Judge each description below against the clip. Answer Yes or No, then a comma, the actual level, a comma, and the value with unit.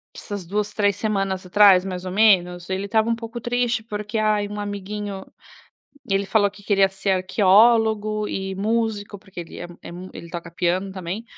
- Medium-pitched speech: No, high, 205 Hz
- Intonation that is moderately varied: No, narrow, 2.2 semitones